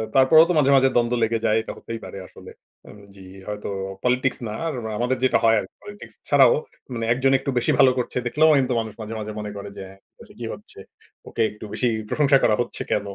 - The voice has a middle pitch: No, low, 120 Hz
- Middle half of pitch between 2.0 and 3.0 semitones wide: No, average, 3.7 semitones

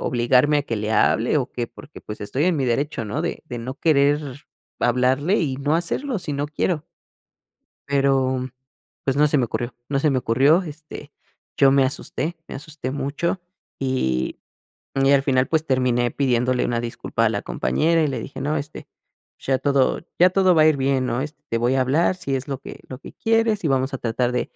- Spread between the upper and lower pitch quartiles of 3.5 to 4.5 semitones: No, average, 2.9 semitones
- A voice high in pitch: No, low, 135 Hz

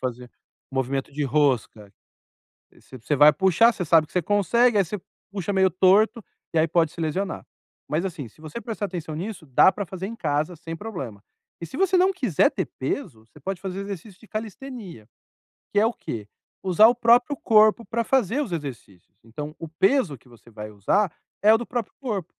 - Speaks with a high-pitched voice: No, medium, 180 Hz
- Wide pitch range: Yes, wide, 6.7 semitones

